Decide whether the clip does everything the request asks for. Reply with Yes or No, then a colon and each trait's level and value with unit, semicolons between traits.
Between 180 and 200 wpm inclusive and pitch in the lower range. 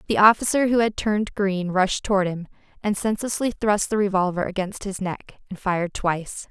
No: average, 185 wpm; high, 200 Hz